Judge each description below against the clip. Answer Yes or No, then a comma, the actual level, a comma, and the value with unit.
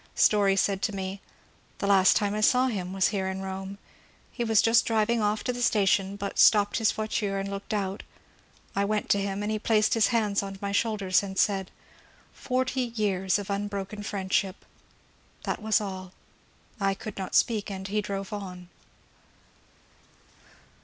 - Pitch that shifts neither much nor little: No, narrow, 1.8 semitones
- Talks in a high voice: Yes, high, 200 Hz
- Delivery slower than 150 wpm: No, average, 180 wpm